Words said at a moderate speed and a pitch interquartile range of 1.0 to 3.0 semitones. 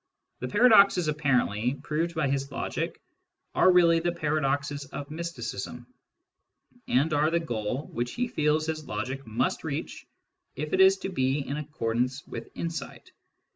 No: average, 160 wpm; average, 4.2 semitones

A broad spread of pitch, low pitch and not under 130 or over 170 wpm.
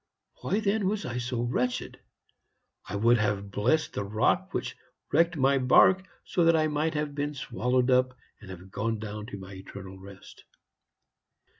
Yes: wide, 6.5 semitones; low, 125 Hz; average, 165 wpm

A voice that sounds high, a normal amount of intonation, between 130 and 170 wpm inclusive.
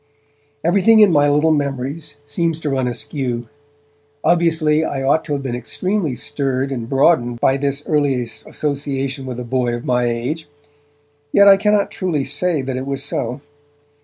No: medium, 140 Hz; average, 3.6 semitones; average, 165 wpm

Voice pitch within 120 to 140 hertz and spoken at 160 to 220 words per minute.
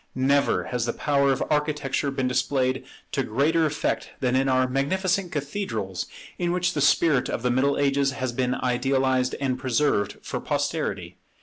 Yes: low, 135 Hz; average, 165 wpm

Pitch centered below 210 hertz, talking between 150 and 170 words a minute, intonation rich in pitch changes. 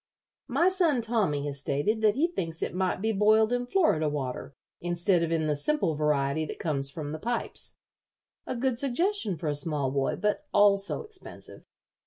No: high, 190 Hz; average, 180 wpm; wide, 8.3 semitones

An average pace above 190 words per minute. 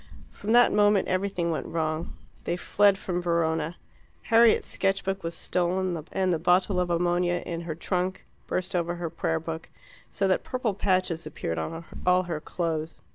No: average, 170 wpm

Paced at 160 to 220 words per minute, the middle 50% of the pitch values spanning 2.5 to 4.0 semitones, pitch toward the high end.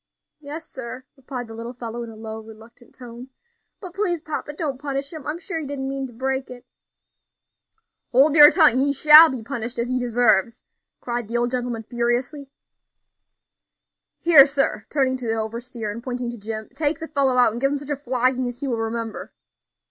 Yes: average, 195 wpm; average, 3.2 semitones; very high, 255 Hz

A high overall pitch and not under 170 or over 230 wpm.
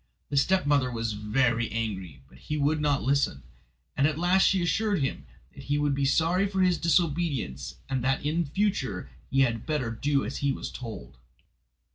No: medium, 140 Hz; average, 180 wpm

